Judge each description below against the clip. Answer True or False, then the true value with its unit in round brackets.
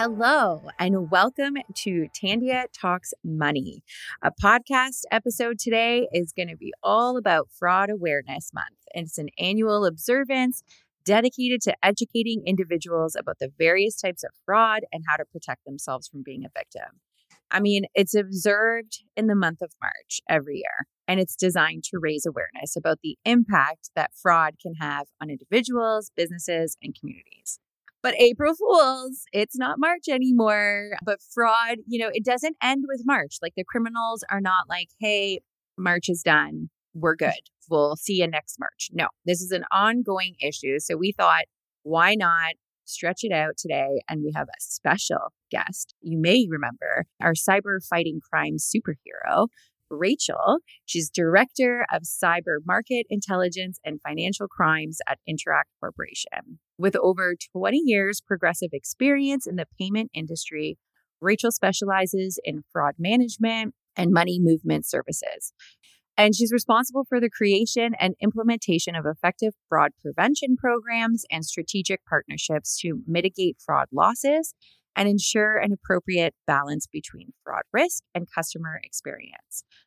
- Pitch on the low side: False (190 Hz)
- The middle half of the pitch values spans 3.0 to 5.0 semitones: False (5.5 semitones)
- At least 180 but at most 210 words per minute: False (150 wpm)